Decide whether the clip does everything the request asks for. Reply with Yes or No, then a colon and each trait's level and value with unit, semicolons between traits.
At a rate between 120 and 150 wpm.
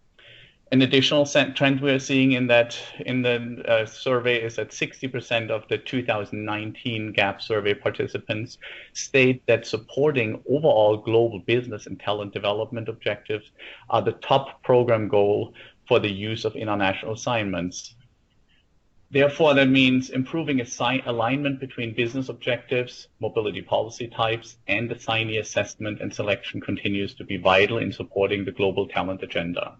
Yes: average, 140 wpm